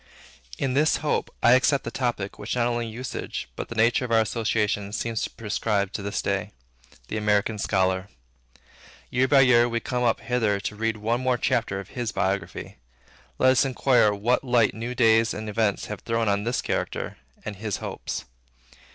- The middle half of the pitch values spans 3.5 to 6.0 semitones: No, average, 2.9 semitones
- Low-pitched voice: Yes, low, 115 Hz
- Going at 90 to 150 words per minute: No, average, 185 wpm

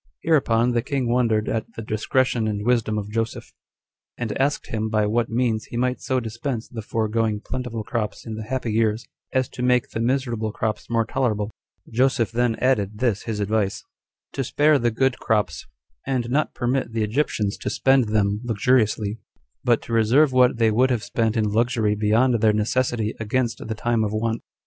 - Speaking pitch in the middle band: No, low, 115 Hz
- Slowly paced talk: No, average, 185 wpm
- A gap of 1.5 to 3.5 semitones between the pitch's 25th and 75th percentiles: Yes, narrow, 2.5 semitones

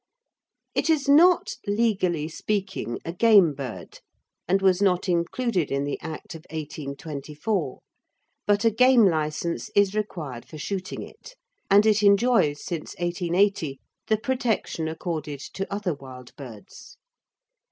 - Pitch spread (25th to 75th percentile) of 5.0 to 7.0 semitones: Yes, wide, 5.5 semitones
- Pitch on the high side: No, medium, 180 Hz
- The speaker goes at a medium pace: No, slow, 130 wpm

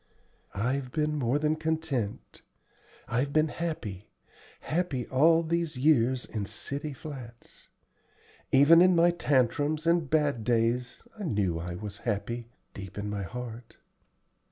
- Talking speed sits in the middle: No, slow, 130 wpm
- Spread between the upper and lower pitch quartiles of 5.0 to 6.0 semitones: Yes, wide, 5.4 semitones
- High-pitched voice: No, low, 130 Hz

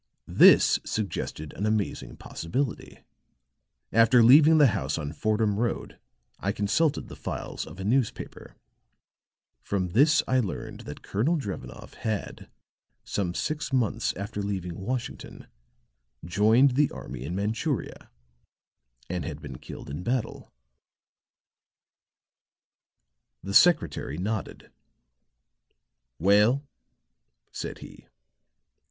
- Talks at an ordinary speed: No, slow, 105 wpm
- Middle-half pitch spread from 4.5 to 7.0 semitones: Yes, average, 5.1 semitones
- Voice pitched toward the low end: Yes, low, 110 Hz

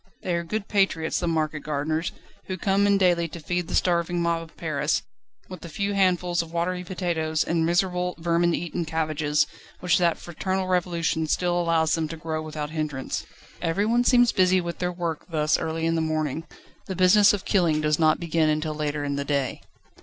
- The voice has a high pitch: No, medium, 170 Hz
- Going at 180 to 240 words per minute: Yes, average, 190 wpm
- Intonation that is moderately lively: No, narrow, 2.3 semitones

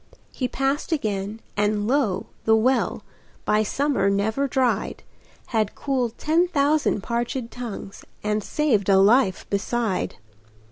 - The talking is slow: Yes, slow, 125 wpm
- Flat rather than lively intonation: No, average, 4.7 semitones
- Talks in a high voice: Yes, high, 230 Hz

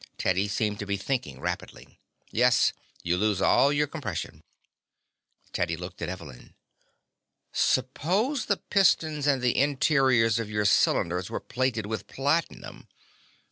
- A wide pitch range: Yes, wide, 6.4 semitones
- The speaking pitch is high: No, low, 115 Hz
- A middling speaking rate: No, slow, 130 wpm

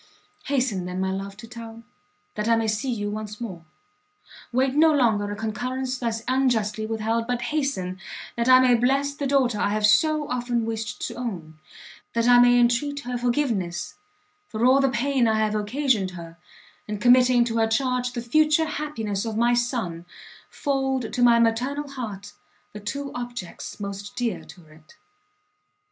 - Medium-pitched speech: No, high, 235 Hz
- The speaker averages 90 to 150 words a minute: No, average, 170 wpm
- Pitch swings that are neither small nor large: Yes, average, 3.5 semitones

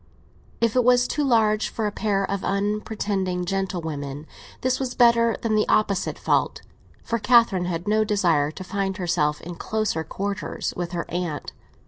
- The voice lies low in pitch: No, high, 200 Hz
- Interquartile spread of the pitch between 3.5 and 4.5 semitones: Yes, average, 3.8 semitones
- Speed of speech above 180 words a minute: No, average, 160 wpm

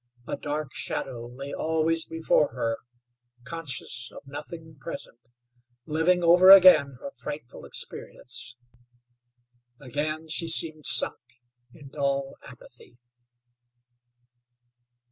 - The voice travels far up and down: No, average, 4.1 semitones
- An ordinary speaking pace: No, slow, 95 wpm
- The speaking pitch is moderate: Yes, medium, 150 Hz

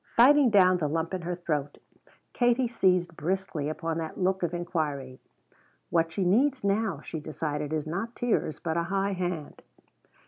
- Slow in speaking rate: No, average, 165 wpm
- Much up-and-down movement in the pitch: No, average, 3.8 semitones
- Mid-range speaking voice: Yes, medium, 175 Hz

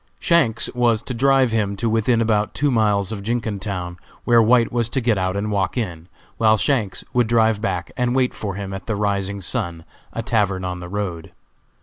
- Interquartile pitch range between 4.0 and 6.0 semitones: No, average, 3.3 semitones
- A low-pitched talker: Yes, low, 110 Hz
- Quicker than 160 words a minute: Yes, average, 200 wpm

